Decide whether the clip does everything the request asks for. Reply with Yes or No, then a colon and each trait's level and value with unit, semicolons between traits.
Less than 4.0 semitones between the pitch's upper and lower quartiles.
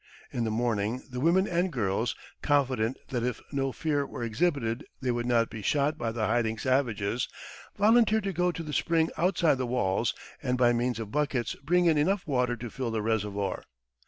No: average, 5.1 semitones